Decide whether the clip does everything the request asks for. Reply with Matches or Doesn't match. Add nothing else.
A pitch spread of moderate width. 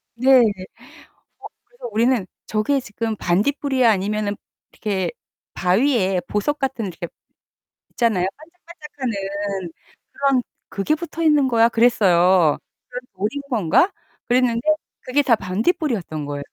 Doesn't match